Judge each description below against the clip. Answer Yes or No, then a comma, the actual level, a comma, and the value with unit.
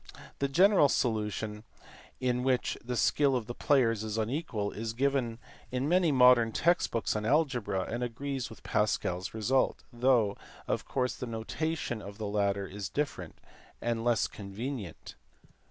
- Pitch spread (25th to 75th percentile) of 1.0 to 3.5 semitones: No, average, 4.0 semitones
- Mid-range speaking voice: No, low, 120 Hz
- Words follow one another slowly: No, average, 155 wpm